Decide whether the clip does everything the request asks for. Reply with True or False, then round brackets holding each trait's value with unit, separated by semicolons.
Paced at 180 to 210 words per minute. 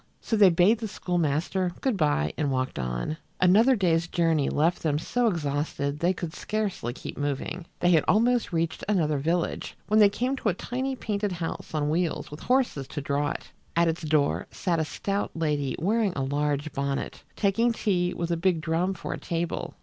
True (190 wpm)